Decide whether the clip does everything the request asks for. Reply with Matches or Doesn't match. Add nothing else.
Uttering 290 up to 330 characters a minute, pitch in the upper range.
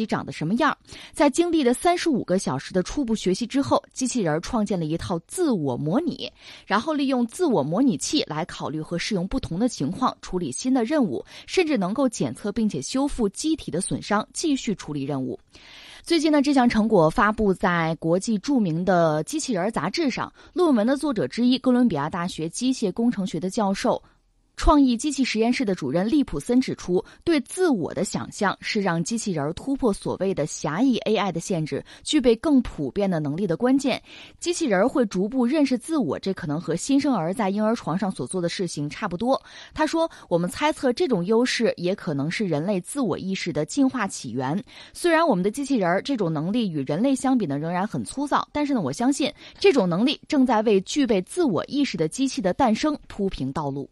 Matches